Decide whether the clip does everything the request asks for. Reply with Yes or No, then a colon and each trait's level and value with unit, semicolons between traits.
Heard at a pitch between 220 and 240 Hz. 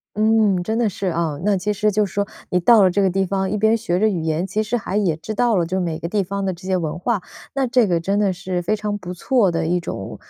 No: high, 195 Hz